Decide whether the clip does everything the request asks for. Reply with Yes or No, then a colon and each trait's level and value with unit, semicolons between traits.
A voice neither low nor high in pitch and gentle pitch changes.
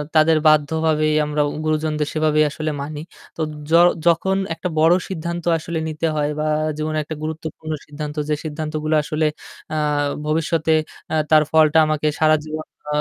Yes: medium, 155 Hz; narrow, 0.7 semitones